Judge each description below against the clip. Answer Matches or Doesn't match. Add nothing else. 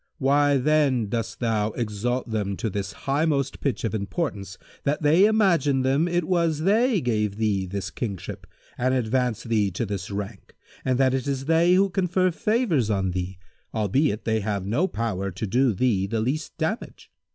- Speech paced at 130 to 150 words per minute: Doesn't match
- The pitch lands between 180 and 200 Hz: Doesn't match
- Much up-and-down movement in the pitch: Matches